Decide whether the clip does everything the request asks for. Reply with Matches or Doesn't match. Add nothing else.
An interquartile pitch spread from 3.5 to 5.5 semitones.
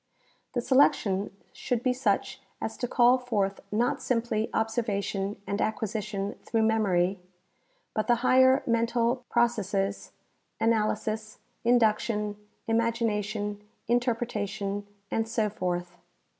Doesn't match